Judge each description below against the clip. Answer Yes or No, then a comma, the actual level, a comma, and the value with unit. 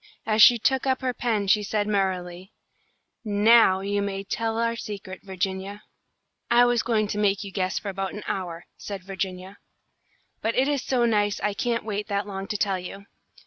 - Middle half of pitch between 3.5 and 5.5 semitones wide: No, average, 2.7 semitones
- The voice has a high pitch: Yes, high, 205 Hz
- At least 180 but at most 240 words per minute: Yes, average, 185 wpm